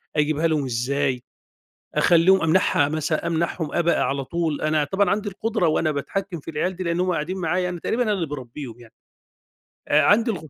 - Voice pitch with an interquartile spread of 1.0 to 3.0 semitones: No, average, 3.9 semitones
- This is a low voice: No, medium, 165 Hz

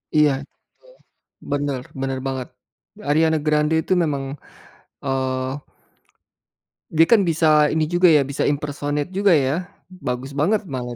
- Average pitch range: Yes, average, 3.2 semitones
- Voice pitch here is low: No, medium, 145 Hz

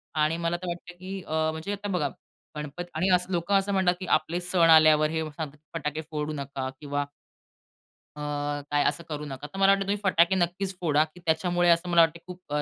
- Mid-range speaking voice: Yes, medium, 165 Hz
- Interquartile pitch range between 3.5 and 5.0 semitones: No, average, 3.1 semitones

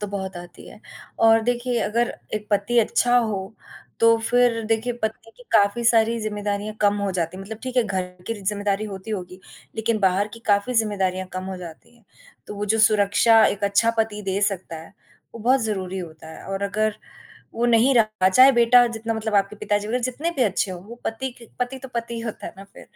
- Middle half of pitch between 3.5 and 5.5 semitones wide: No, average, 2.7 semitones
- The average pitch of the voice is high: Yes, high, 215 Hz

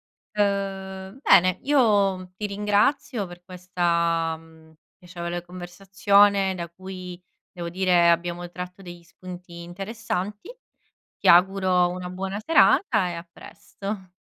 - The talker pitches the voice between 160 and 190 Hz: Yes, medium, 185 Hz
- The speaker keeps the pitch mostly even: Yes, narrow, 2.2 semitones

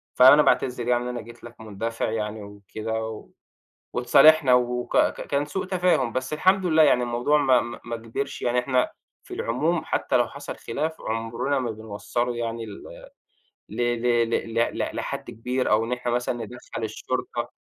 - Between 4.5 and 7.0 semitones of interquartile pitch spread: No, narrow, 2.5 semitones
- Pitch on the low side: Yes, low, 120 Hz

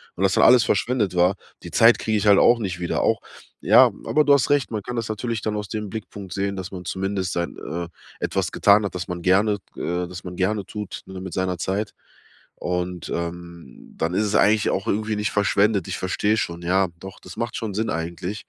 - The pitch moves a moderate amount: Yes, average, 3.0 semitones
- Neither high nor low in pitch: No, low, 100 Hz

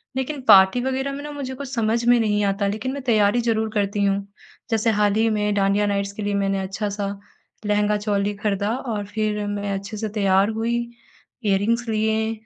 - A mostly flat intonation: Yes, narrow, 2.1 semitones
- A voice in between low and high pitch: No, high, 210 Hz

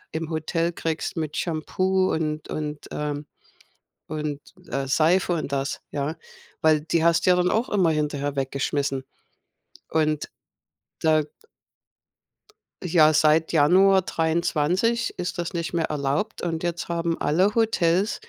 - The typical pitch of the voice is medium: Yes, medium, 160 Hz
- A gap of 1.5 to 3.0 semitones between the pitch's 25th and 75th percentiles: Yes, narrow, 2.6 semitones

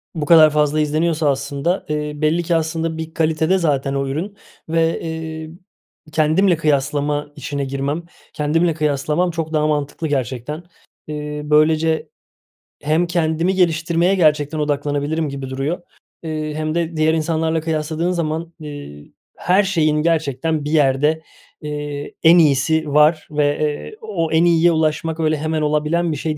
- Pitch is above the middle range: No, medium, 155 Hz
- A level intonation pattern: Yes, narrow, 1.7 semitones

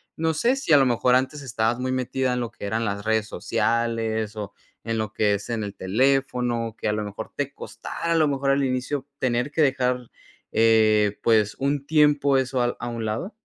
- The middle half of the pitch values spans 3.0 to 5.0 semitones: Yes, average, 3.6 semitones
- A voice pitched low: Yes, low, 120 Hz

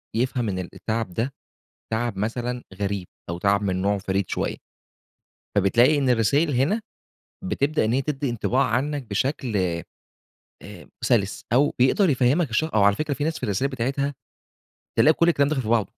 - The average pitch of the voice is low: Yes, low, 125 Hz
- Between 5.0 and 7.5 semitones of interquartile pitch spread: Yes, wide, 5.5 semitones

